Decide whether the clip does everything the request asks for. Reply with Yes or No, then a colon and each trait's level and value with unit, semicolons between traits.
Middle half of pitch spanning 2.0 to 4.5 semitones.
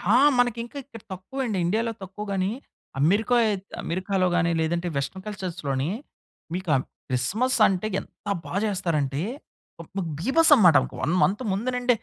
No: average, 4.9 semitones